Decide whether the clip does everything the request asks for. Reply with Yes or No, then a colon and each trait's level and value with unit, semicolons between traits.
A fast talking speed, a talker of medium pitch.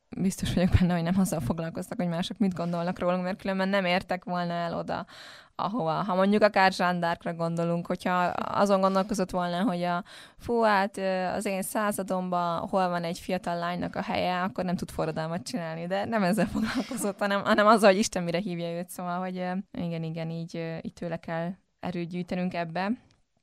Yes: fast, 180 wpm; medium, 180 Hz